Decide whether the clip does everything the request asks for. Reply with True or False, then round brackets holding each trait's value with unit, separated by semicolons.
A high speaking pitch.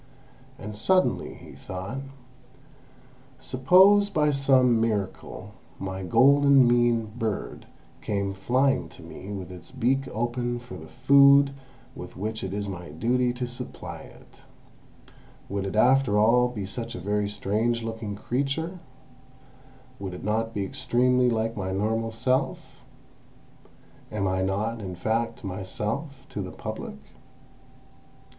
False (115 Hz)